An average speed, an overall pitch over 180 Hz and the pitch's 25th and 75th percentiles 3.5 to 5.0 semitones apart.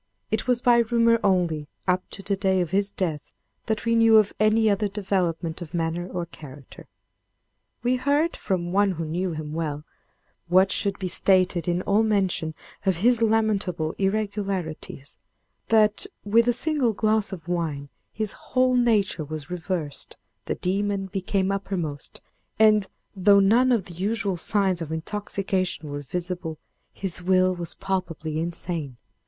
Yes: average, 150 wpm; high, 190 Hz; average, 3.9 semitones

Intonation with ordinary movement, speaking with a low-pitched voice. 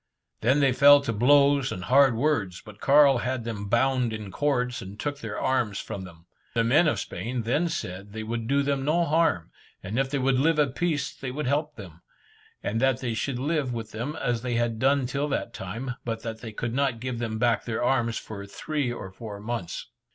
Yes: average, 4.0 semitones; low, 125 Hz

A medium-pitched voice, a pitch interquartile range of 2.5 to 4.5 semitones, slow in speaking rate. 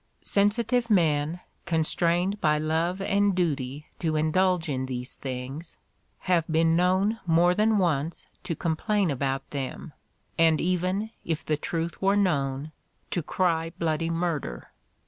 Yes: medium, 165 Hz; average, 3.3 semitones; slow, 130 wpm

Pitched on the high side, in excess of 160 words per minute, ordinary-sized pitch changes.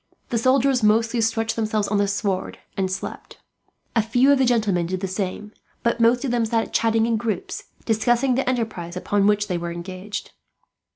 Yes: high, 220 Hz; average, 185 wpm; average, 3.0 semitones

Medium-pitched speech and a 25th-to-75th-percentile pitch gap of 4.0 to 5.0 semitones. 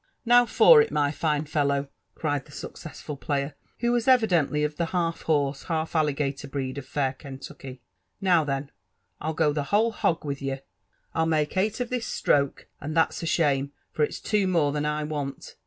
No: medium, 150 Hz; average, 3.1 semitones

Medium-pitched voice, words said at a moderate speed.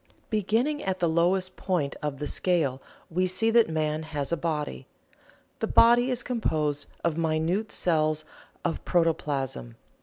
Yes: medium, 165 Hz; average, 145 wpm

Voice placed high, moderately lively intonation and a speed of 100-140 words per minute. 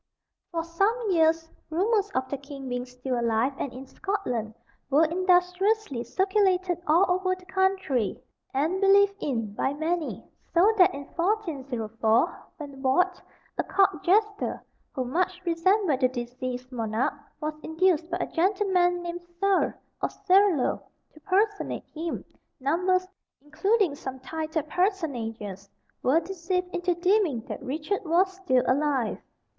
No: very high, 330 Hz; wide, 6.1 semitones; slow, 135 wpm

